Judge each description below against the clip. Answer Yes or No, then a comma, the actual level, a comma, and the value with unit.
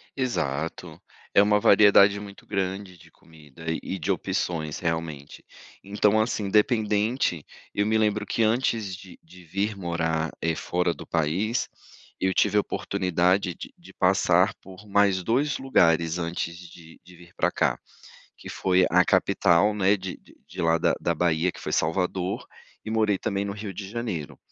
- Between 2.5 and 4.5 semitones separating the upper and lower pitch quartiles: Yes, average, 3.6 semitones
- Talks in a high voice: No, very low, 95 Hz